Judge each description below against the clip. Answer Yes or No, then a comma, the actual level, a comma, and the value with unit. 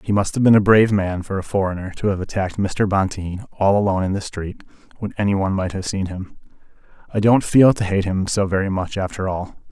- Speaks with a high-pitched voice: No, low, 100 Hz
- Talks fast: Yes, fast, 230 wpm